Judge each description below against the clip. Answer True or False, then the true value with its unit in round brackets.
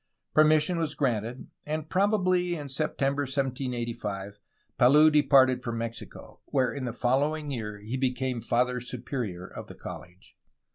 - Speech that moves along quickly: False (140 wpm)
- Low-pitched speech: True (130 Hz)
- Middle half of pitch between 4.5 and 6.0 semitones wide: False (4.1 semitones)